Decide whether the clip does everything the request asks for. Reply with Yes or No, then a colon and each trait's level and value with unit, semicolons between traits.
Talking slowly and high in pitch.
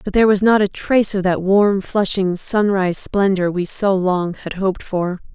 No: average, 200 wpm; high, 195 Hz